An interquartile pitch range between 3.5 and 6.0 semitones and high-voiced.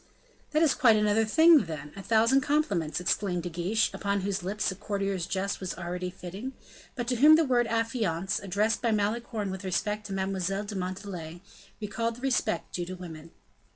Yes: average, 3.9 semitones; high, 200 Hz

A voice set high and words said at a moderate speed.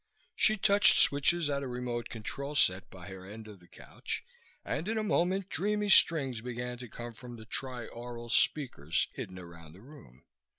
No: low, 125 Hz; average, 175 wpm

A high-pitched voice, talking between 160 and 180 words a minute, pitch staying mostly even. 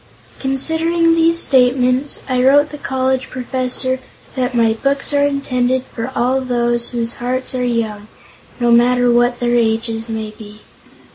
No: very high, 250 Hz; average, 145 wpm; narrow, 2.0 semitones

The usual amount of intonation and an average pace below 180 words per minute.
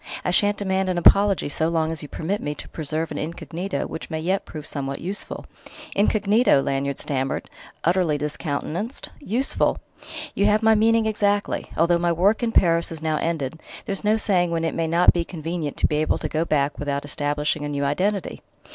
No: average, 4.9 semitones; average, 190 wpm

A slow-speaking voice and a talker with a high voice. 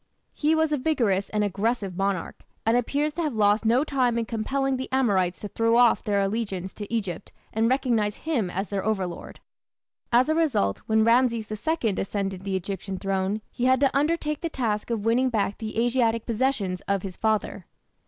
No: average, 185 wpm; high, 225 Hz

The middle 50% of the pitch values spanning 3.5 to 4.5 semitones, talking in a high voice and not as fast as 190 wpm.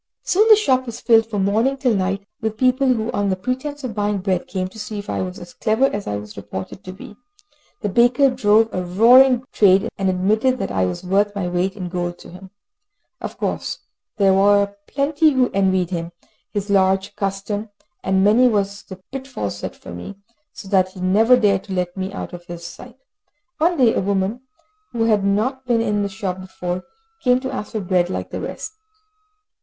No: average, 4.2 semitones; high, 200 Hz; fast, 205 wpm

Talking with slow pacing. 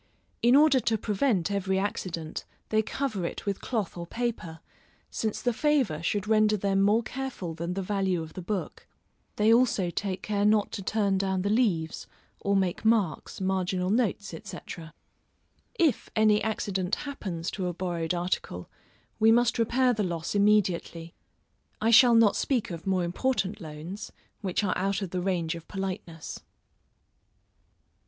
No: average, 155 wpm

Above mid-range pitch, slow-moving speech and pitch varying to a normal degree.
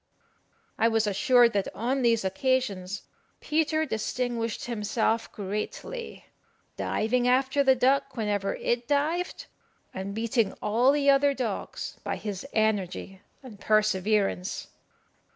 Yes: high, 230 Hz; slow, 115 wpm; average, 4.1 semitones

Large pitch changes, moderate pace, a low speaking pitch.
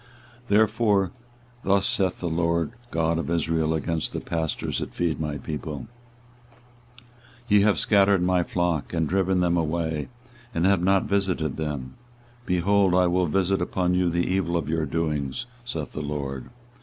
No: average, 3.2 semitones; average, 155 wpm; very low, 85 Hz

